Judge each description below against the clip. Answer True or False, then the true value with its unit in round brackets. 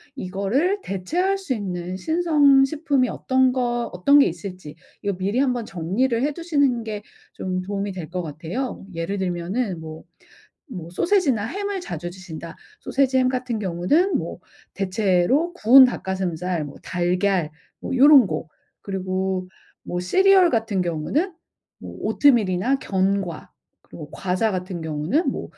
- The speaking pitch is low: False (200 Hz)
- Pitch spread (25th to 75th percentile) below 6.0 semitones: False (6.9 semitones)